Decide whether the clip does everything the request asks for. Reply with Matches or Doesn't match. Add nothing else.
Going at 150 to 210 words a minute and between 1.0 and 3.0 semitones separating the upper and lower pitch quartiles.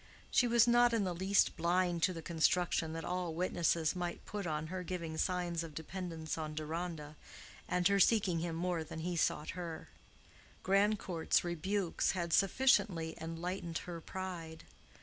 Matches